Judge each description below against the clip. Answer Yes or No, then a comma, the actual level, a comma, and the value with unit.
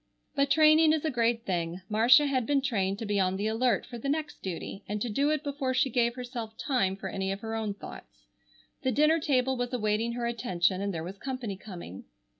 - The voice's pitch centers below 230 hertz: No, high, 235 Hz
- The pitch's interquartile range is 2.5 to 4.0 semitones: No, average, 5.1 semitones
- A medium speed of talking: No, fast, 225 wpm